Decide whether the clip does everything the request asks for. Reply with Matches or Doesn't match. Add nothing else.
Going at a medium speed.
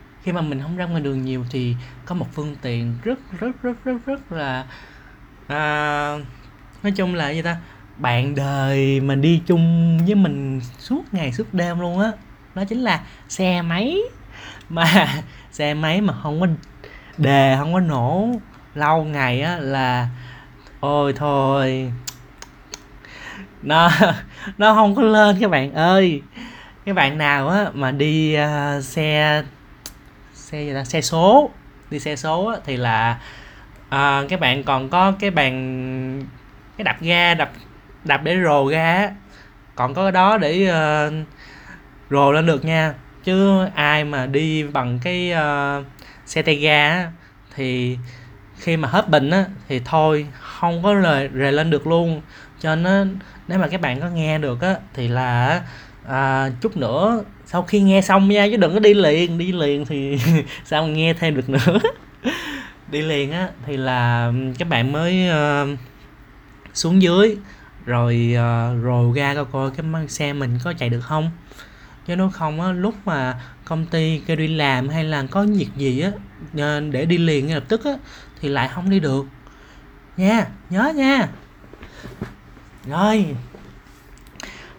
Doesn't match